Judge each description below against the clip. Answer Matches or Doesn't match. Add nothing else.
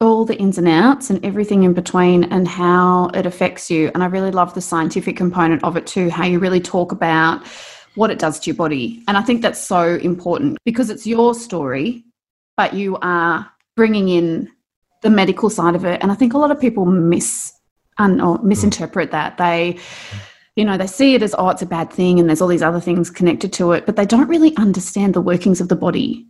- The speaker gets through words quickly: Matches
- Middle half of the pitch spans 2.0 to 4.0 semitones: Matches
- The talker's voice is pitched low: Doesn't match